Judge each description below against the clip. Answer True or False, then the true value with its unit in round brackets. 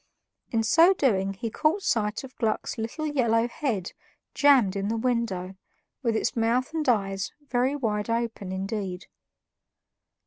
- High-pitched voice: True (230 Hz)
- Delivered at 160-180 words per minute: False (140 wpm)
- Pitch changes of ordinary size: True (4.3 semitones)